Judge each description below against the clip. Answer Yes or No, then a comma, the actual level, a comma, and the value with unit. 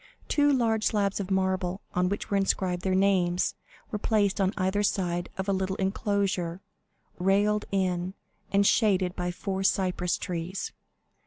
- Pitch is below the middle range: No, high, 190 Hz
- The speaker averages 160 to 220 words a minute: No, average, 150 wpm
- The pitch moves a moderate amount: No, narrow, 1.8 semitones